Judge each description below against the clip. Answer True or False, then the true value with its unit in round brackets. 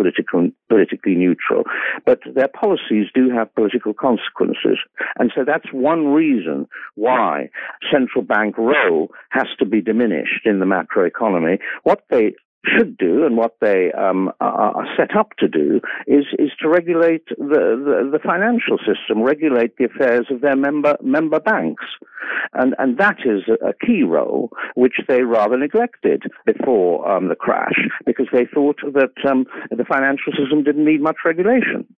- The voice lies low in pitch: False (150 Hz)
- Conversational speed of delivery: True (155 wpm)